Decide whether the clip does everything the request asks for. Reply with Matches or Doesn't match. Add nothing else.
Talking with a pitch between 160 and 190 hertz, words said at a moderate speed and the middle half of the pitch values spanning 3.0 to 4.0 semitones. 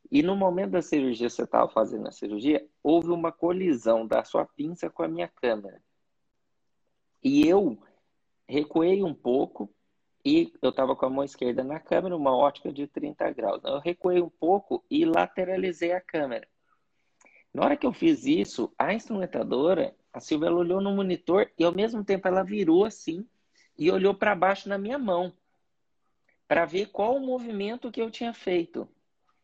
Doesn't match